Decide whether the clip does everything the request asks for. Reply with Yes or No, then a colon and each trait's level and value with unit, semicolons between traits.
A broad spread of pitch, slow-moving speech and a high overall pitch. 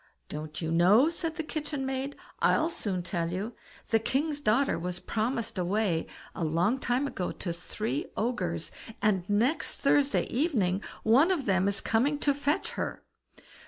No: wide, 7.6 semitones; average, 160 wpm; high, 220 Hz